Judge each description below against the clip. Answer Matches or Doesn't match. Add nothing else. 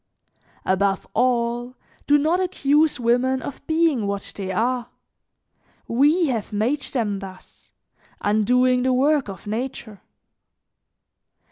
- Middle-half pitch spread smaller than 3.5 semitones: Doesn't match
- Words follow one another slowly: Matches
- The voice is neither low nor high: Doesn't match